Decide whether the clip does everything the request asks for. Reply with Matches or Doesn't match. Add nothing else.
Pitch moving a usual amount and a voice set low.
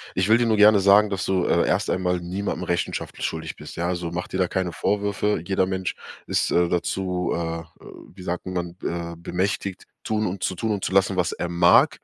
Doesn't match